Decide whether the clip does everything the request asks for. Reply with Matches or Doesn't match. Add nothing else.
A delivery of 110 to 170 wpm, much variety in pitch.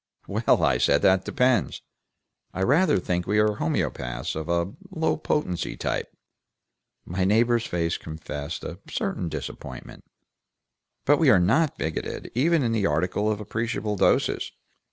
Matches